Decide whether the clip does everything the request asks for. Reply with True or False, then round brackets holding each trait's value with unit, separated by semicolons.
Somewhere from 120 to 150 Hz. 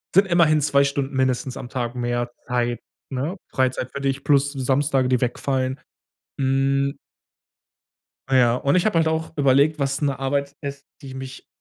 True (135 Hz)